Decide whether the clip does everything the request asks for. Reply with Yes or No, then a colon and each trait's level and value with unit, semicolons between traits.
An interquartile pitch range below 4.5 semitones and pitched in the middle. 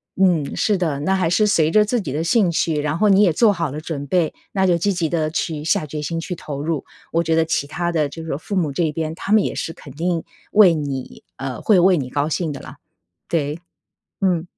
Yes: average, 3.4 semitones; medium, 165 Hz